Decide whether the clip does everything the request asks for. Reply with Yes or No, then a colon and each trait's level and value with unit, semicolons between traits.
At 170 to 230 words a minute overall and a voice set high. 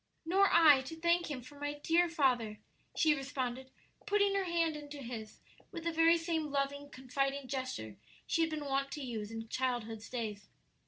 Yes: average, 175 wpm; very high, 285 Hz